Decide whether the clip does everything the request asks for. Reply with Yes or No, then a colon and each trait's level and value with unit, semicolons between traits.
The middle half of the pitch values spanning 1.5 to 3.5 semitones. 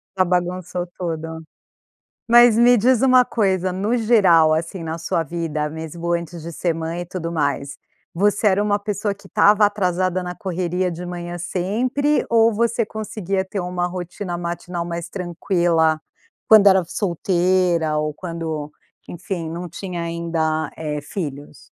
Yes: average, 3.1 semitones